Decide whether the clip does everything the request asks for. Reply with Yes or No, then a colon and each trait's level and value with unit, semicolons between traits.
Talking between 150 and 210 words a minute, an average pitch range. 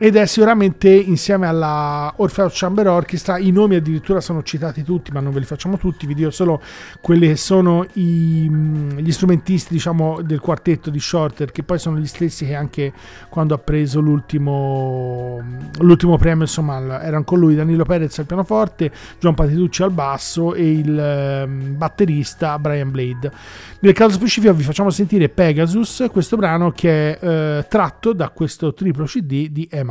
Yes: average, 165 wpm; average, 3.5 semitones